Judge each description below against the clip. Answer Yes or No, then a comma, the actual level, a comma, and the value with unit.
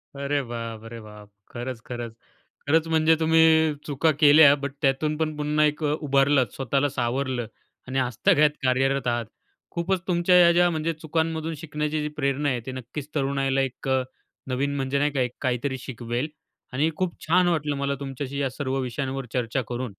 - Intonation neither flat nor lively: Yes, average, 3.0 semitones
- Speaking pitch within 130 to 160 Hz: Yes, medium, 140 Hz